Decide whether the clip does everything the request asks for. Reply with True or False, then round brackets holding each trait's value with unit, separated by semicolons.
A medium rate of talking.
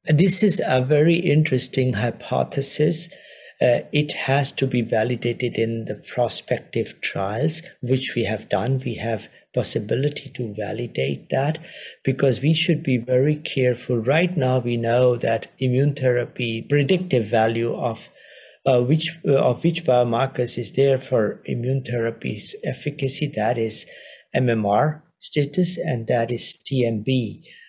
False (130 wpm)